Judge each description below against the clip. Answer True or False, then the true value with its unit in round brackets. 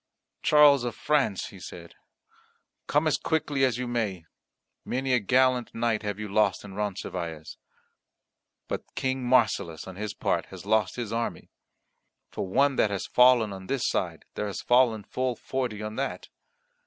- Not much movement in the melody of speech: False (4.2 semitones)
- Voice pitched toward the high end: False (115 Hz)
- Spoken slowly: False (160 wpm)